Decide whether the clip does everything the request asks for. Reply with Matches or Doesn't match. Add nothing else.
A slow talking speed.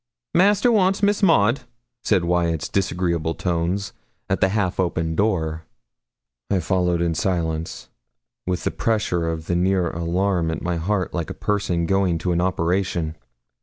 Doesn't match